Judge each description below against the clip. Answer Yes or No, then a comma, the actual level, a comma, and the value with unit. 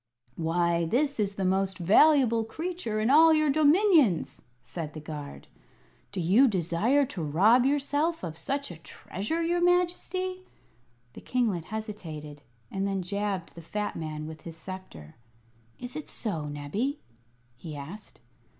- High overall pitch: Yes, high, 205 Hz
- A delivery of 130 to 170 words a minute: Yes, average, 140 wpm